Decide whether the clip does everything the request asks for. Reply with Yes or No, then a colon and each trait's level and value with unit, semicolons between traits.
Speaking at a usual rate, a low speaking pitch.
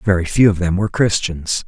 No: fast, 215 wpm; very low, 95 Hz